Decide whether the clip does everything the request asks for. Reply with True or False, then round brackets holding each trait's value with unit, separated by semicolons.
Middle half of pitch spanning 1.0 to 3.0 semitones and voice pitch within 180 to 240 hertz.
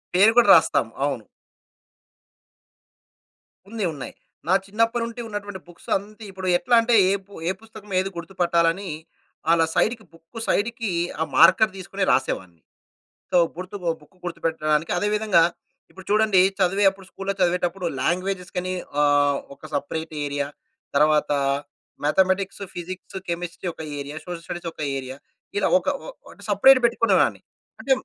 False (3.6 semitones; 185 Hz)